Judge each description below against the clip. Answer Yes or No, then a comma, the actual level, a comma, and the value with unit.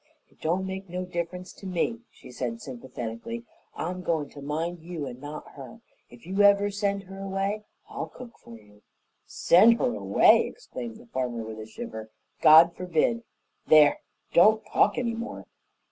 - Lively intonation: Yes, wide, 6.6 semitones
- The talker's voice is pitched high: No, medium, 175 Hz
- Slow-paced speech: No, average, 165 wpm